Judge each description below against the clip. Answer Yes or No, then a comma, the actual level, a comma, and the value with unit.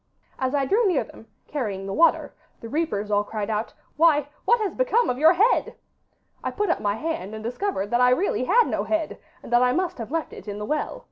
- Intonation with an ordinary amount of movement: No, wide, 7.9 semitones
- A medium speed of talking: No, fast, 230 wpm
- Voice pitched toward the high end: Yes, very high, 280 Hz